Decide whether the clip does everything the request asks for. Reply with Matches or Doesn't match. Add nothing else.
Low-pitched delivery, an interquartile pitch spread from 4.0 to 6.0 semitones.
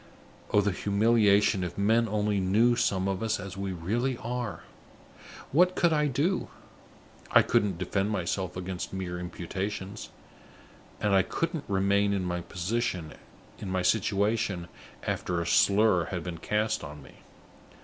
Doesn't match